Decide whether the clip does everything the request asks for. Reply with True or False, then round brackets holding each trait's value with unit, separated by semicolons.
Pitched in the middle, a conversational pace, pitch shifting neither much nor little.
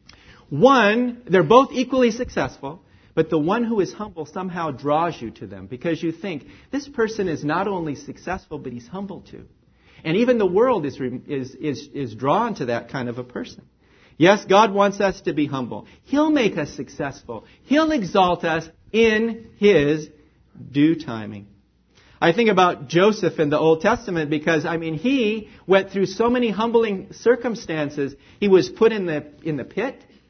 False (170 Hz; 175 wpm; 6.7 semitones)